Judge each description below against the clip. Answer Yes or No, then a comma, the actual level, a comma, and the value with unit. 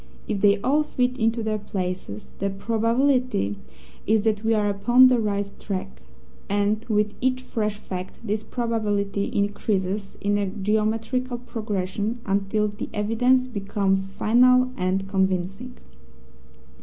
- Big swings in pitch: No, average, 2.8 semitones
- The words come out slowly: Yes, slow, 130 wpm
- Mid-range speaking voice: No, high, 210 Hz